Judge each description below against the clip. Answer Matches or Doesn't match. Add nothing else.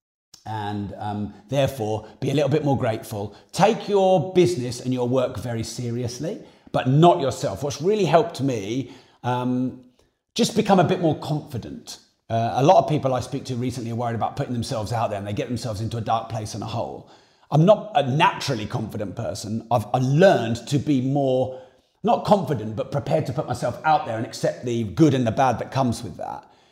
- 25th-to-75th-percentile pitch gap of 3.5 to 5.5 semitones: Matches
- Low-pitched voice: Matches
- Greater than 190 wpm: Matches